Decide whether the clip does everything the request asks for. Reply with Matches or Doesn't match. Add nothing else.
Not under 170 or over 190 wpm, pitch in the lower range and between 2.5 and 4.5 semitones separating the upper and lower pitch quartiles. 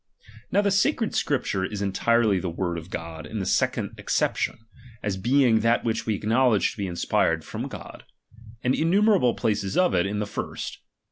Doesn't match